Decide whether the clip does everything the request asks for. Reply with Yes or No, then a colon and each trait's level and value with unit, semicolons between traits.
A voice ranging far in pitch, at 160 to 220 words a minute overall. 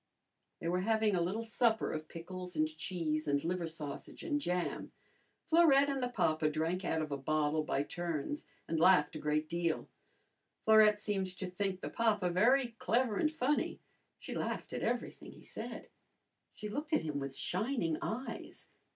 Yes: wide, 6.1 semitones; average, 170 wpm